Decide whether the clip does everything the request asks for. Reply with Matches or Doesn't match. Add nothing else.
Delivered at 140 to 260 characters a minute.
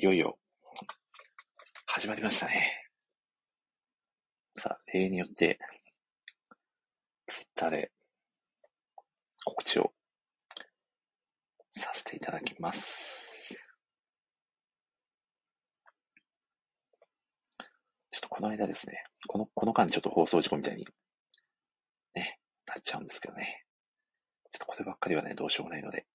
Matches